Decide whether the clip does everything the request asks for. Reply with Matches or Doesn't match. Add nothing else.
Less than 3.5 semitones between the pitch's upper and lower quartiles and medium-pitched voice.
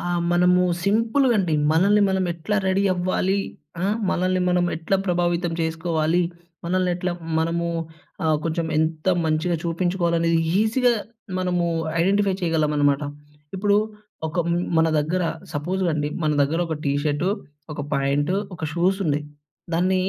Matches